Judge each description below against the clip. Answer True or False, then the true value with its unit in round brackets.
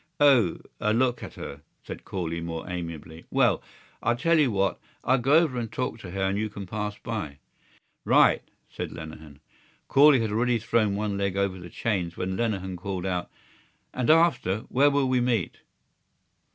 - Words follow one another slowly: False (175 wpm)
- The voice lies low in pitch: True (105 Hz)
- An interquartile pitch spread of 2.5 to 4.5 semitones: False (5.3 semitones)